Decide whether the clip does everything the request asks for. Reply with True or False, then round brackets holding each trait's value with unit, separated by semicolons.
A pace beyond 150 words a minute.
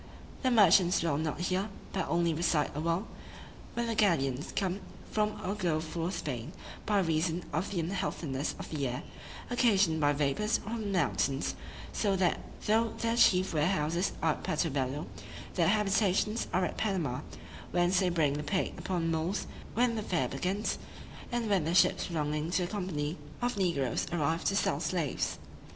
True (170 wpm)